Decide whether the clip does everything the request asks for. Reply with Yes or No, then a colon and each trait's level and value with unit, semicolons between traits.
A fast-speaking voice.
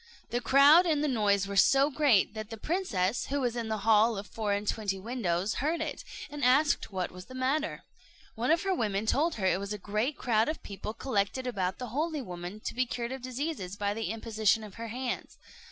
Yes: fast, 220 wpm